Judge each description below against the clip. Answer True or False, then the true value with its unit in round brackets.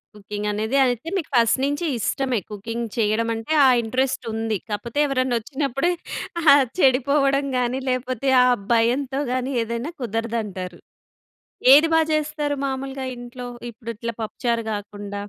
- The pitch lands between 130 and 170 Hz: False (240 Hz)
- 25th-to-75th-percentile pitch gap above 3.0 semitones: True (3.4 semitones)